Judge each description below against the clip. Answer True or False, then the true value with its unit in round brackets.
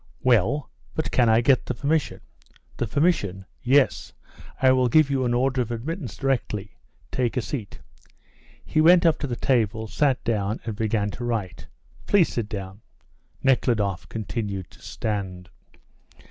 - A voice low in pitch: True (120 Hz)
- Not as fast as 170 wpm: True (150 wpm)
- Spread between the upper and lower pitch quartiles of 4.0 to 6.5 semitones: True (4.4 semitones)